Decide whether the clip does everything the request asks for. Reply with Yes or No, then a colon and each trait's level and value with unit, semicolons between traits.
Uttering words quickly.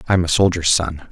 Yes: fast, 215 wpm